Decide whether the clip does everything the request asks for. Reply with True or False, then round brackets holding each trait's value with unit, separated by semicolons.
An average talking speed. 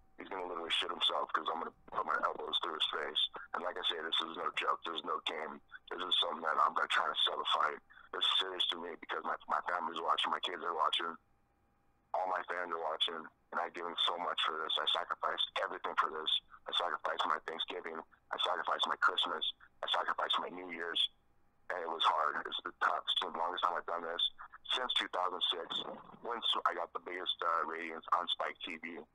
False (230 wpm)